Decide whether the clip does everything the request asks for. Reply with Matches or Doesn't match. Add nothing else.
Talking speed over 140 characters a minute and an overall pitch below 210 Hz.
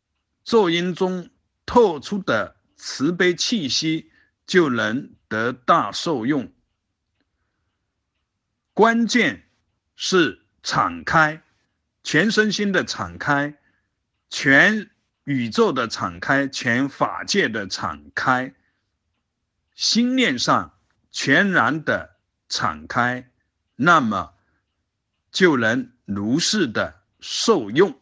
Doesn't match